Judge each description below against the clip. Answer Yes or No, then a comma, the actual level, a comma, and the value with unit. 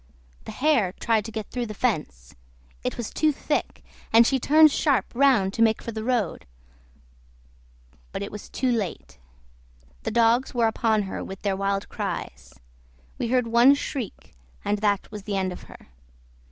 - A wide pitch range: No, average, 3.8 semitones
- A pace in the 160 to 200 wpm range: Yes, average, 170 wpm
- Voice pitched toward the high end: Yes, high, 225 Hz